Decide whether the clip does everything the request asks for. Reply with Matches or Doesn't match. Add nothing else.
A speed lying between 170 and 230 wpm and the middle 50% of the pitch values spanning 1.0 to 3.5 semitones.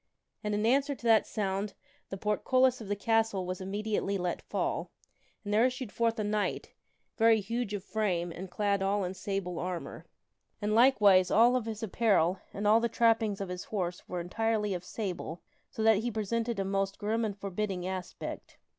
Matches